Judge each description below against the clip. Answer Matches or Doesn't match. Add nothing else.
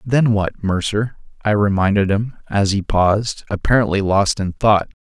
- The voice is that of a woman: Doesn't match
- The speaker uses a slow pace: Doesn't match